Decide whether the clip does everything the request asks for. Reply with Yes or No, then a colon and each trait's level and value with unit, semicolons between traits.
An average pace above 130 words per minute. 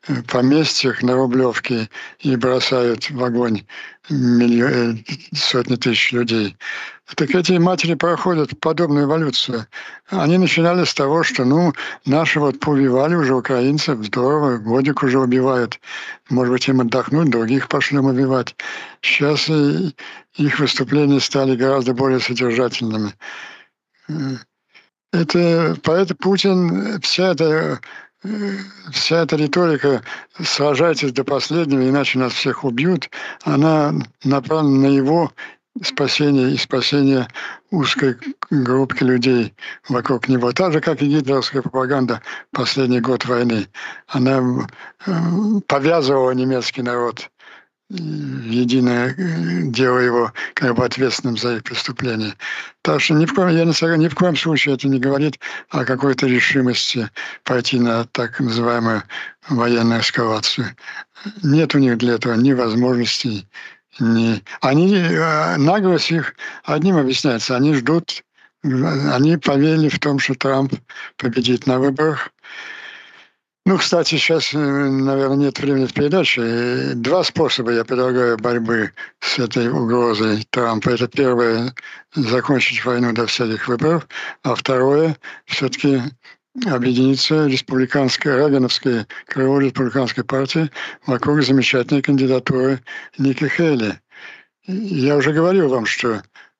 No: average, 115 wpm